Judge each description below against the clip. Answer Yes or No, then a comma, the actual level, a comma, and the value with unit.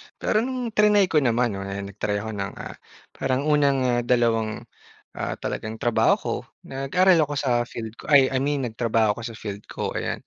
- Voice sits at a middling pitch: No, low, 120 Hz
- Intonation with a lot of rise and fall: No, average, 4.7 semitones